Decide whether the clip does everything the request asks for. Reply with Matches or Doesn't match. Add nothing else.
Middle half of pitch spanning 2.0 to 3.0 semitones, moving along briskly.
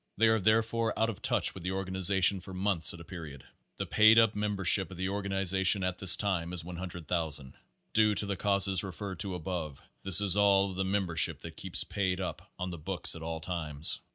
Matches